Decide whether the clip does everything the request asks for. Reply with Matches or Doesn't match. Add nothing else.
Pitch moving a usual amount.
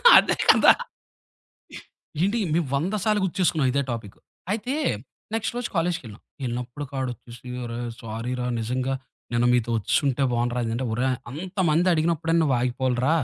Doesn't match